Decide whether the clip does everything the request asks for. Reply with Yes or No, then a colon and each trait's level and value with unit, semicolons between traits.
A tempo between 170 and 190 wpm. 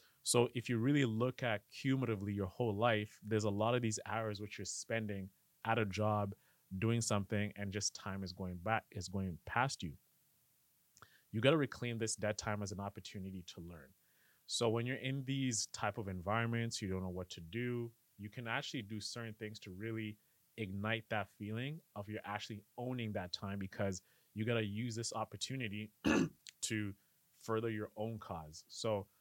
Yes: average, 185 wpm